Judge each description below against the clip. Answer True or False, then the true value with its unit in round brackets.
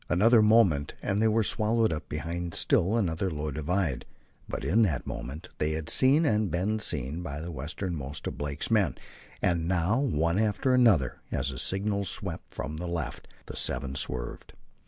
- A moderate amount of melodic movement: False (5.9 semitones)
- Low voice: True (85 Hz)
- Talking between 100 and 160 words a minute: False (175 wpm)